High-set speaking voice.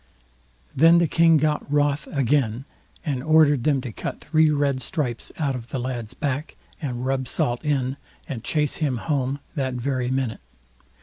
No: medium, 140 Hz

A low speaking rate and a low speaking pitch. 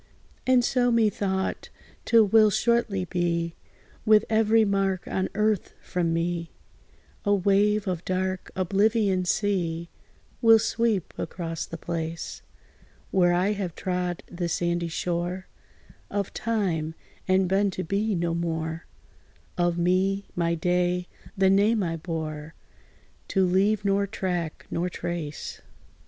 No: slow, 125 wpm; medium, 185 Hz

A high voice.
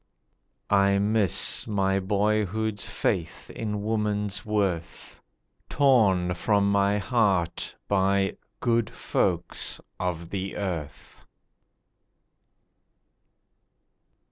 No: low, 100 Hz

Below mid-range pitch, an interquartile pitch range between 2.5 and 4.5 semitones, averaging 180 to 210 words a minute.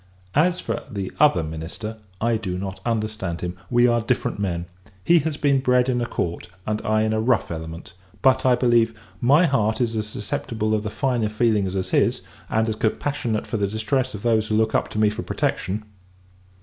Yes: low, 110 Hz; average, 2.8 semitones; average, 200 wpm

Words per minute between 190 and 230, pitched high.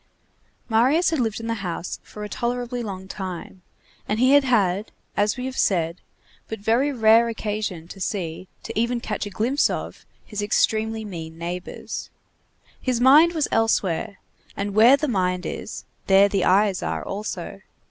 No: average, 165 wpm; high, 215 Hz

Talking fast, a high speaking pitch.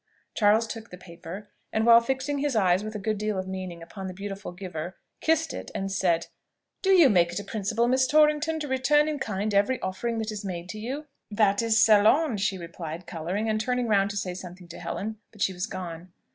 Yes: fast, 215 wpm; high, 205 Hz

